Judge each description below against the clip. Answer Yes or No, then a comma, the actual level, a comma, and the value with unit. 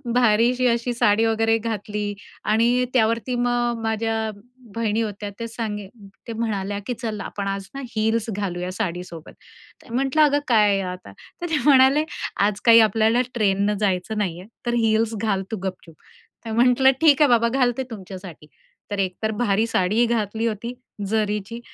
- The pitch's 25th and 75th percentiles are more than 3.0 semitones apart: No, average, 2.7 semitones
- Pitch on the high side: Yes, high, 220 Hz